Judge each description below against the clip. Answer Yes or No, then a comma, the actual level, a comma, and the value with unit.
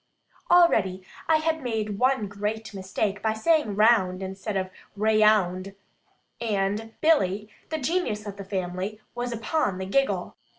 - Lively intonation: No, average, 3.7 semitones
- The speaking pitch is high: Yes, high, 215 Hz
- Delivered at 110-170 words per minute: Yes, slow, 135 wpm